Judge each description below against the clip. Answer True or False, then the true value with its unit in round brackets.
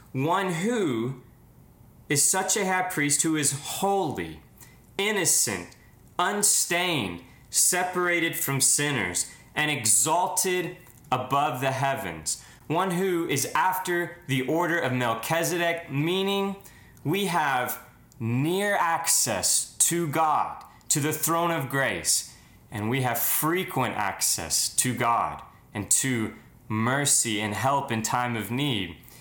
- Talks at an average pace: False (115 wpm)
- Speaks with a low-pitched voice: False (145 Hz)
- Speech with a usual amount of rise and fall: False (6.3 semitones)